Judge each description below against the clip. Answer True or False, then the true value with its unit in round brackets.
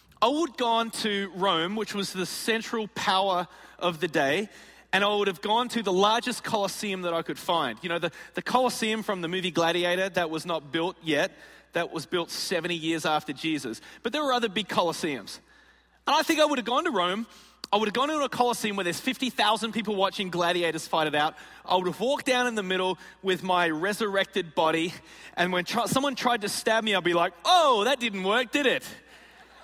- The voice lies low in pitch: False (195 Hz)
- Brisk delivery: True (220 wpm)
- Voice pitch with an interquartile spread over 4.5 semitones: True (4.9 semitones)